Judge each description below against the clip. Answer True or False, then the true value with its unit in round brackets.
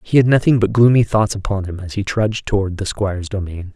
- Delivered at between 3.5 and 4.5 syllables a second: False (6.0 syllables/s)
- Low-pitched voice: True (100 Hz)